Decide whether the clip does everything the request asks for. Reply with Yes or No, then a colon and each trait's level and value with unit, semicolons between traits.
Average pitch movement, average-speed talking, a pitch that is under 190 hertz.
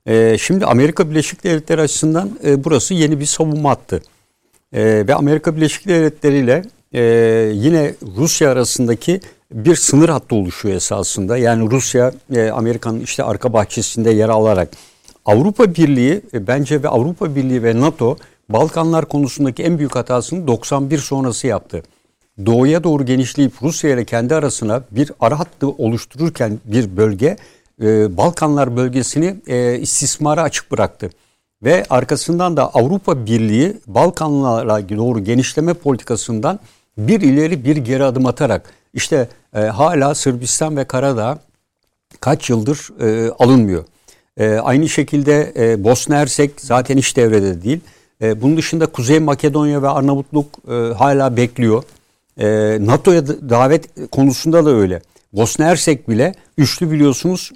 Yes: average, 4.9 semitones; average, 125 wpm; low, 135 Hz